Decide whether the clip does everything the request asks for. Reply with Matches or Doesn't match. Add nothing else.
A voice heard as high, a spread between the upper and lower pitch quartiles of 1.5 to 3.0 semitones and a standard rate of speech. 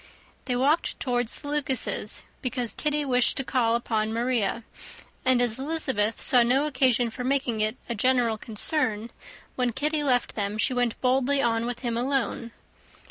Matches